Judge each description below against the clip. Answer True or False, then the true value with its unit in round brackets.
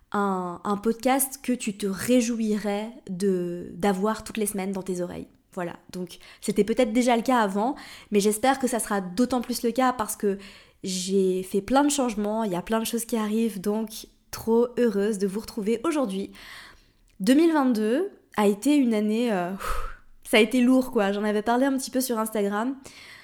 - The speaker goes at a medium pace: True (190 wpm)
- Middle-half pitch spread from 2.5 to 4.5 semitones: True (3.6 semitones)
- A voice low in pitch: False (220 Hz)